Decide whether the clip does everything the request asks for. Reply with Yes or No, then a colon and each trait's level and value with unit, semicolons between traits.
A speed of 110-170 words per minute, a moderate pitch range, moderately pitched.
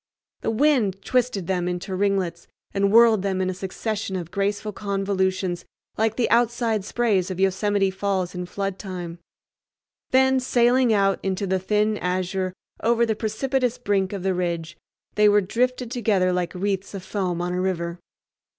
No: average, 160 wpm; average, 3.0 semitones; high, 195 Hz